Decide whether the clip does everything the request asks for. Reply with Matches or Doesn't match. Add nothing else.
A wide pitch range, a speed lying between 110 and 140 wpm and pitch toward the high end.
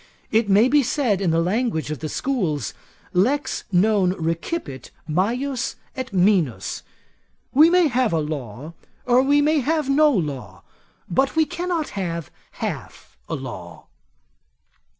Matches